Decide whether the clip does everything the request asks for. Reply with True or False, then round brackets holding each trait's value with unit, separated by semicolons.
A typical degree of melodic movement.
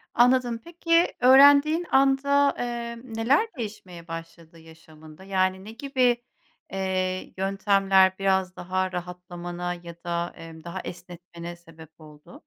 False (5.8 semitones)